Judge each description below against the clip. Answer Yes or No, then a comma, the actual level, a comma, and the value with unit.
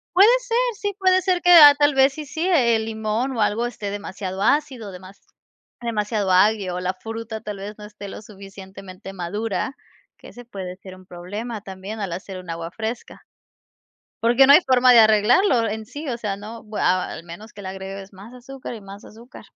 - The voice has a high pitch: Yes, high, 215 Hz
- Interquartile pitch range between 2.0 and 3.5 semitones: No, average, 4.1 semitones